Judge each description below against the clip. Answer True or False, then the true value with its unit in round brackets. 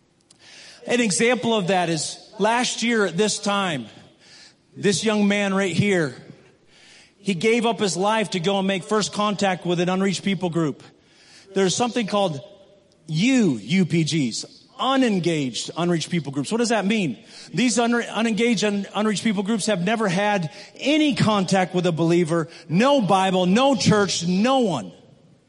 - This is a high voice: True (200 Hz)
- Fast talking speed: False (155 wpm)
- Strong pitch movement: False (3.7 semitones)